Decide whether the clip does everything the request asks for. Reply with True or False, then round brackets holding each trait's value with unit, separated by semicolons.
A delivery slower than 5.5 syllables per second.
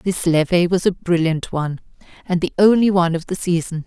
False (5.7 syllables/s)